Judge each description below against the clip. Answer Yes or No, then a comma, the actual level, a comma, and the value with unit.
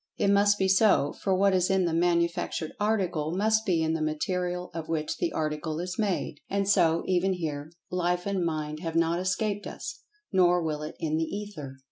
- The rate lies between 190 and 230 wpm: Yes, average, 195 wpm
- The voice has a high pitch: No, medium, 175 Hz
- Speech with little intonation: No, average, 3.3 semitones